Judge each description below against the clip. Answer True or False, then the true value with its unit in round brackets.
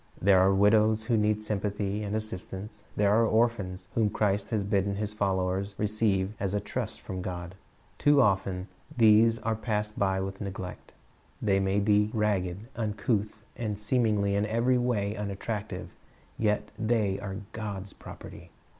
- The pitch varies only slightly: True (1.9 semitones)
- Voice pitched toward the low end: True (105 Hz)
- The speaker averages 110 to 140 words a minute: False (150 wpm)